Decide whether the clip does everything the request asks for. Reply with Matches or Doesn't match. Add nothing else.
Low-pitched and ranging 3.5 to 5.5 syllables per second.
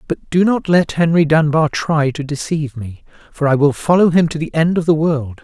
Doesn't match